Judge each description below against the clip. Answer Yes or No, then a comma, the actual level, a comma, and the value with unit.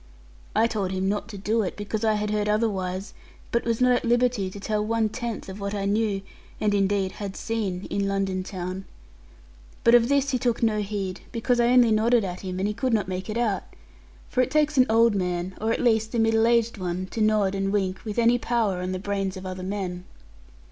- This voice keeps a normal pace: No, fast, 225 wpm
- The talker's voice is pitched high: Yes, high, 210 Hz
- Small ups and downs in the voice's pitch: No, average, 3.2 semitones